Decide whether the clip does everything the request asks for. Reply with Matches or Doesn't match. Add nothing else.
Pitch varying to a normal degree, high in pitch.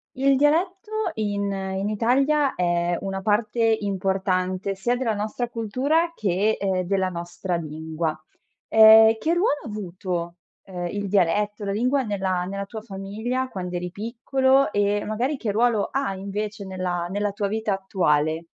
Matches